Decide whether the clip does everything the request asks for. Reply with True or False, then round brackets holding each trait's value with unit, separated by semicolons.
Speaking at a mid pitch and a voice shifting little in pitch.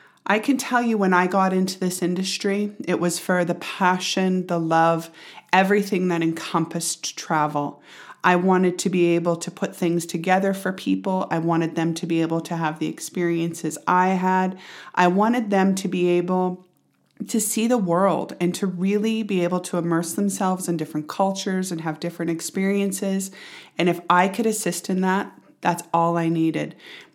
True (180 Hz; 2.2 semitones)